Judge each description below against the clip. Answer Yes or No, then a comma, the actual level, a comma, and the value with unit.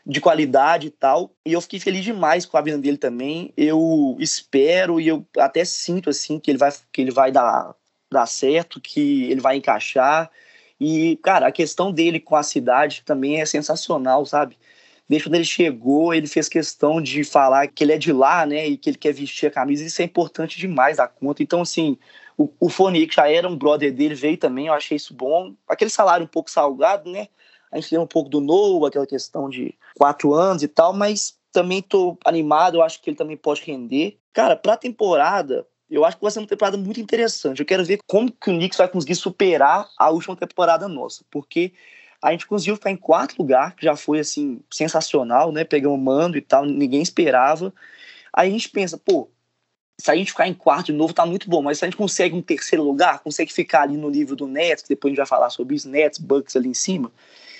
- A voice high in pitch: No, medium, 160 Hz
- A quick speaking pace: Yes, fast, 220 wpm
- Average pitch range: Yes, average, 4.4 semitones